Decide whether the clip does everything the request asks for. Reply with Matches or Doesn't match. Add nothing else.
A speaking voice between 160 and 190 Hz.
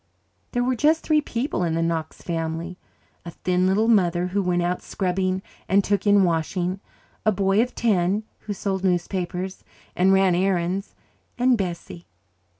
Matches